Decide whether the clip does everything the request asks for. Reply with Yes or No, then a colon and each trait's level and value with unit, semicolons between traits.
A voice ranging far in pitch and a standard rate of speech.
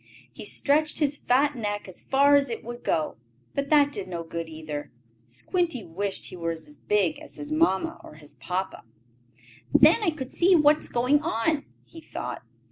Yes: wide, 8.7 semitones; average, 185 wpm